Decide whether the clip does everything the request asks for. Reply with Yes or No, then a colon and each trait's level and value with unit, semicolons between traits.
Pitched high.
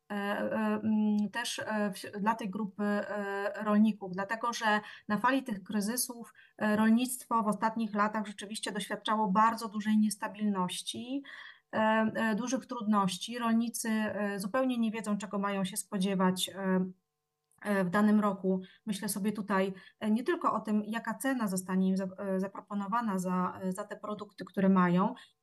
Yes: high, 210 Hz